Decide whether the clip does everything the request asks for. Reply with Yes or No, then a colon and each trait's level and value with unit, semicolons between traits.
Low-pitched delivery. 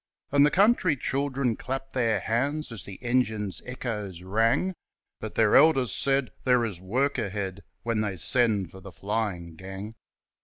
Yes: low, 115 Hz